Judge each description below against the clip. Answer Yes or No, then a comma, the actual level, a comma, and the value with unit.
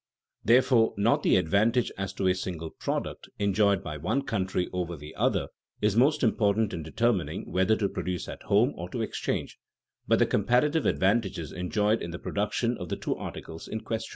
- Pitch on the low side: Yes, low, 100 Hz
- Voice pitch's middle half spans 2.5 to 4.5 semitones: Yes, average, 3.9 semitones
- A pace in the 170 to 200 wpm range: Yes, average, 180 wpm